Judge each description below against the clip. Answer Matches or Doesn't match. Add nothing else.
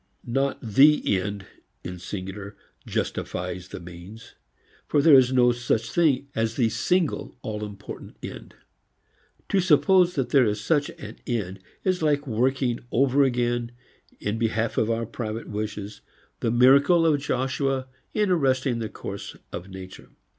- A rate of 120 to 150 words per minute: Matches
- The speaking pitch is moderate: Doesn't match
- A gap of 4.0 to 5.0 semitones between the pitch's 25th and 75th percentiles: Matches